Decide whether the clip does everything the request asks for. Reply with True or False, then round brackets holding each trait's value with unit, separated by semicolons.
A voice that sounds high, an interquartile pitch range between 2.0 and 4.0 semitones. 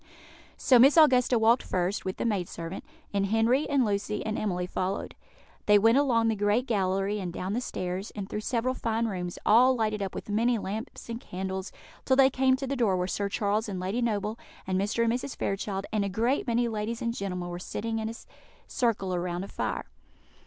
True (215 Hz; 3.5 semitones)